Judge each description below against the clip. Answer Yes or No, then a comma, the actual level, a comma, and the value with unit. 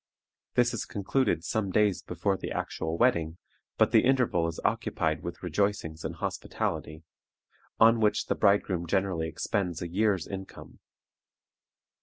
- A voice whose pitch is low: Yes, very low, 95 Hz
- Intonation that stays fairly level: No, average, 4.1 semitones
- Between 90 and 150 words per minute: Yes, slow, 135 wpm